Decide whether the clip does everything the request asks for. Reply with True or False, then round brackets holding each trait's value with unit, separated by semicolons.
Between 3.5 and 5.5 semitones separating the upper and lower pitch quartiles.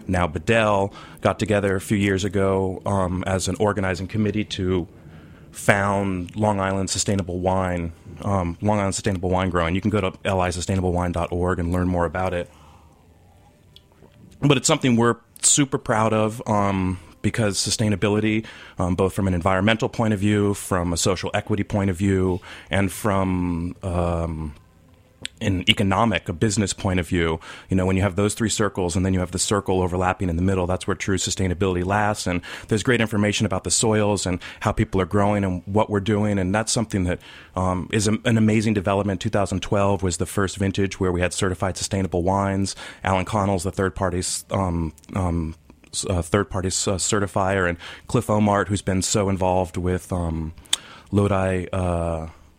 False (2.4 semitones)